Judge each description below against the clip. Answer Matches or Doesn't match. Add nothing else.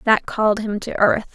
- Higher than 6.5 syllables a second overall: Doesn't match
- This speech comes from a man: Doesn't match